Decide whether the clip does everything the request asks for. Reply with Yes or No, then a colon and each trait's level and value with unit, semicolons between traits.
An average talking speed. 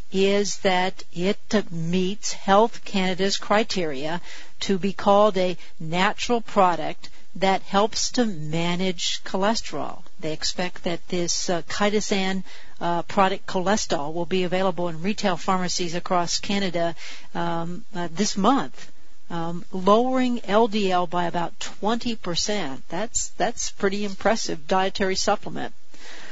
No: slow, 115 wpm